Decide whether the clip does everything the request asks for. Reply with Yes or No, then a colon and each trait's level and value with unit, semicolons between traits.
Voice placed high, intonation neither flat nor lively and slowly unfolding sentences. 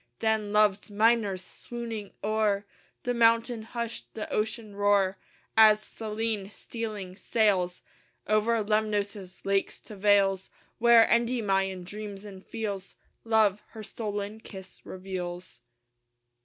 No: high, 210 Hz; narrow, 2.2 semitones; slow, 110 wpm